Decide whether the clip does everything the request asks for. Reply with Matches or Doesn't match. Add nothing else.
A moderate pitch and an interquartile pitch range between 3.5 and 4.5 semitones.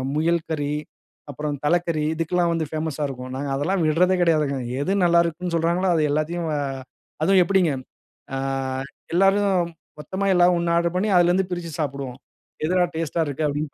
Doesn't match